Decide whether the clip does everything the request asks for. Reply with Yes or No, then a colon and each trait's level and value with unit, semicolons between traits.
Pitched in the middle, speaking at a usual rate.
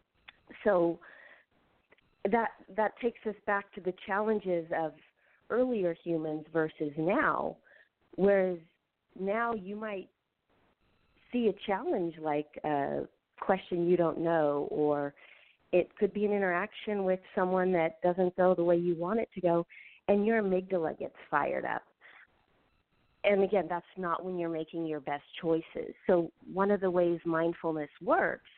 Yes: medium, 180 Hz; average, 145 wpm